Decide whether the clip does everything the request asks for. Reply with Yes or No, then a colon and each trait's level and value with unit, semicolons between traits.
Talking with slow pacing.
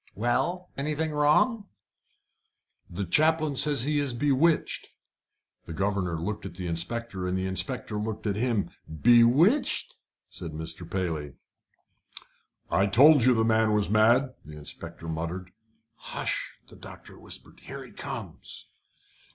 Yes: slow, 130 wpm